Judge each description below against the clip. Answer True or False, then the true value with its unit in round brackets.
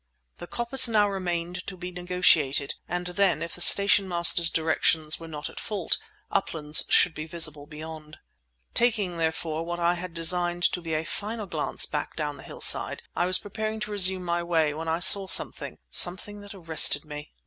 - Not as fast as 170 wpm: False (180 wpm)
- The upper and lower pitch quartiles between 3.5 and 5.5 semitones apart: False (2.8 semitones)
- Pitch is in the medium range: True (175 Hz)